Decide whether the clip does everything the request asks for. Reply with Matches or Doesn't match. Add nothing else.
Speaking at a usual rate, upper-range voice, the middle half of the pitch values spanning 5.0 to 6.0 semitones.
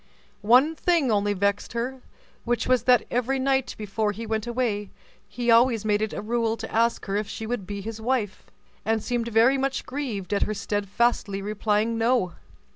Doesn't match